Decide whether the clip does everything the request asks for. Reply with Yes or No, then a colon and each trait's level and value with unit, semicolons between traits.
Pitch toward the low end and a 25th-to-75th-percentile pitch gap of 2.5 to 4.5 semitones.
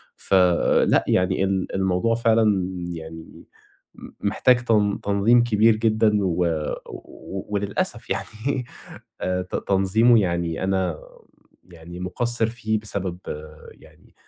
Yes: low, 100 Hz; average, 3.5 semitones